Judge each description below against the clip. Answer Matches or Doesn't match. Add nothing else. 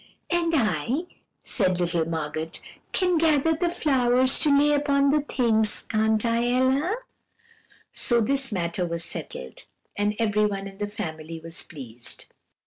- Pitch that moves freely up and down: Matches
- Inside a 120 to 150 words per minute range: Matches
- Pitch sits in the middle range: Doesn't match